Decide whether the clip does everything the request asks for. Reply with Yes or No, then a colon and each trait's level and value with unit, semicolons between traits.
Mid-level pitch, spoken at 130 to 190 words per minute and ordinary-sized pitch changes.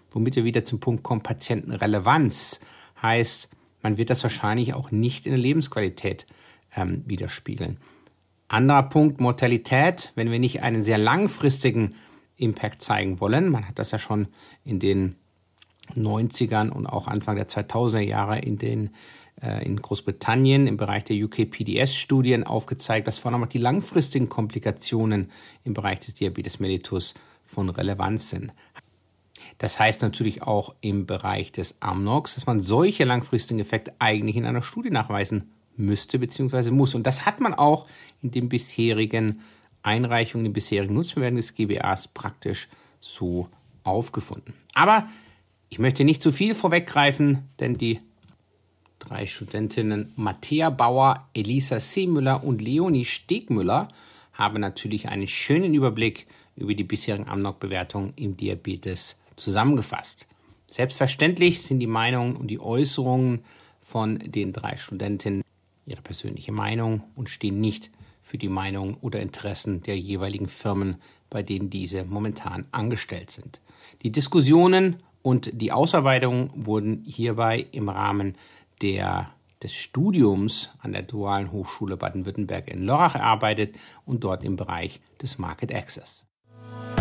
No: low, 110 Hz; slow, 135 wpm; average, 4.0 semitones